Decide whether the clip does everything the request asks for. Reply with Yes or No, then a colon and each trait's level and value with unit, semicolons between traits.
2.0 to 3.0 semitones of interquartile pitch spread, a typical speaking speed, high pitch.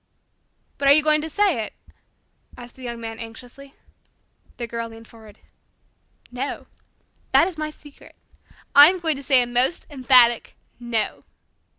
No: average, 4.2 semitones; average, 160 wpm; very high, 255 Hz